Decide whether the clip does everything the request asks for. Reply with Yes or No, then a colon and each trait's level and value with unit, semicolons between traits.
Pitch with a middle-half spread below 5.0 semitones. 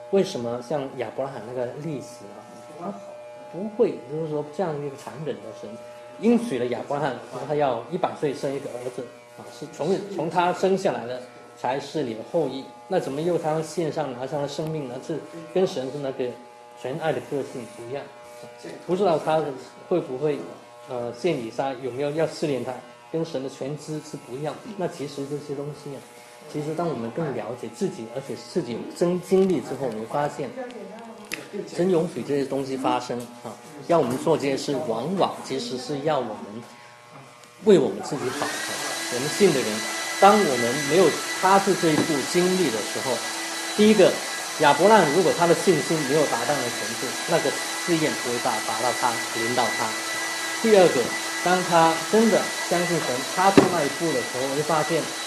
No: wide, 5.6 semitones